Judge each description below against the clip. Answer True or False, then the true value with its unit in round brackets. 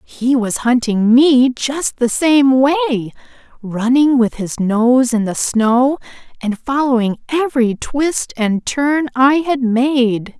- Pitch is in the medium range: False (255 Hz)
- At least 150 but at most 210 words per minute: False (140 wpm)